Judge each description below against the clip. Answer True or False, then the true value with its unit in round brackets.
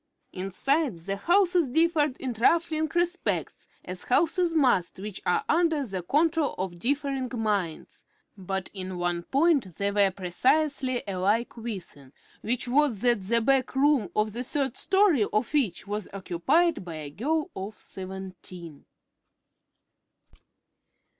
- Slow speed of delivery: True (130 wpm)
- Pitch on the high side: True (235 Hz)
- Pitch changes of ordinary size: False (7.7 semitones)